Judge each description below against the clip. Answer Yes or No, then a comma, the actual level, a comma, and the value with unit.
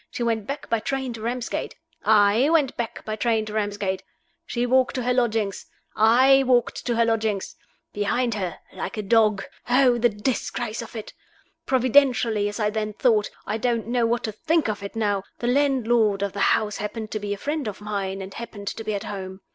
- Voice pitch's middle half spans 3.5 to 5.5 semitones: No, average, 2.9 semitones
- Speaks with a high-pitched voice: Yes, high, 225 Hz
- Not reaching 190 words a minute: No, fast, 205 wpm